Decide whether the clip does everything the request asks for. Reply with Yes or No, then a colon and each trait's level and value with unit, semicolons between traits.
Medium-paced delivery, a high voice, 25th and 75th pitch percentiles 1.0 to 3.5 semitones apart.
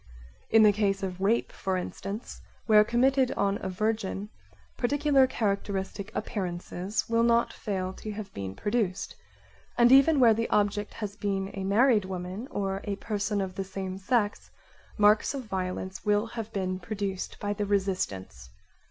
Yes: average, 160 wpm; high, 205 Hz; average, 2.7 semitones